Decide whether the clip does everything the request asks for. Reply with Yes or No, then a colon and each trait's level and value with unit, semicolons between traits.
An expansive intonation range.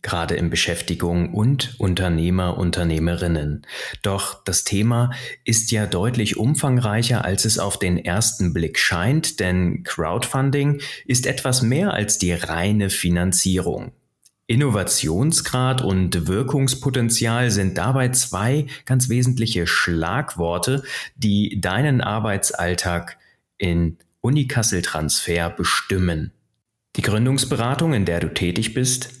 Yes: wide, 6.4 semitones